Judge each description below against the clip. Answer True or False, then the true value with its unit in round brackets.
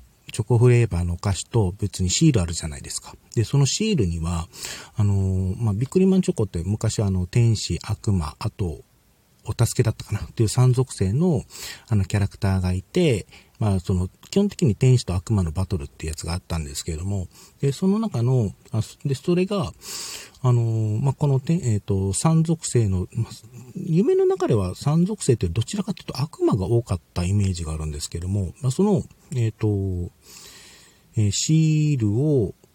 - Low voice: True (110 Hz)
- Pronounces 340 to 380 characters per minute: True (365 characters per minute)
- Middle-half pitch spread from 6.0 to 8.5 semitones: True (6.4 semitones)